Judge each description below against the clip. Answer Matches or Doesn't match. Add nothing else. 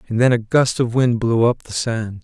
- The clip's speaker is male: Matches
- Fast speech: Matches